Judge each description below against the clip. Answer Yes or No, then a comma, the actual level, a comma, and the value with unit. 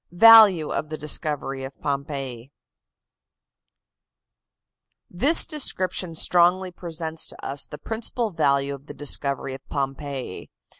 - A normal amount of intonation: Yes, average, 4.6 semitones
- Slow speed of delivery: Yes, slow, 110 wpm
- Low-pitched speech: No, medium, 155 Hz